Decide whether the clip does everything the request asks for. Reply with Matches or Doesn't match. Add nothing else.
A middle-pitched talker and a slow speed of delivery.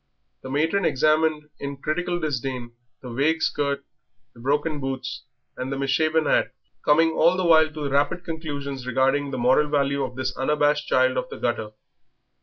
Doesn't match